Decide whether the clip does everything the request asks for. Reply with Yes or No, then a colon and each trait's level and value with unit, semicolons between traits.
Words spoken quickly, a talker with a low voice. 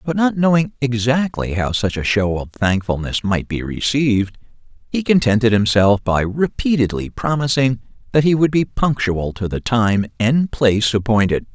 No: average, 155 wpm; low, 120 Hz